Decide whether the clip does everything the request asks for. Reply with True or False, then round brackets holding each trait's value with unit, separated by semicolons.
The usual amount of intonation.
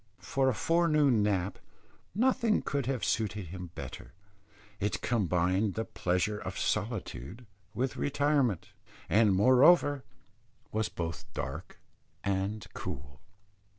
False (6.1 semitones)